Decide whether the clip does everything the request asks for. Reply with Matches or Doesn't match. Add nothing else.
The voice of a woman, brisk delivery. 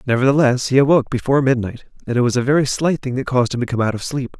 Doesn't match